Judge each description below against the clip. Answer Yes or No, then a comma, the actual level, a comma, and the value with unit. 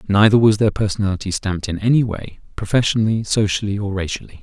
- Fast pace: No, average, 165 wpm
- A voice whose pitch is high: No, low, 100 Hz